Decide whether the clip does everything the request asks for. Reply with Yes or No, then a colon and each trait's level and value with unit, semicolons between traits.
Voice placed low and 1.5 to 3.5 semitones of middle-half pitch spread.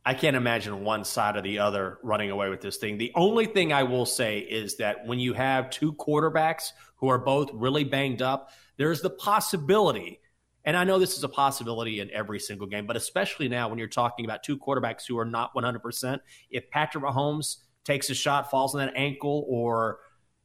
No: low, 130 Hz; average, 4.1 semitones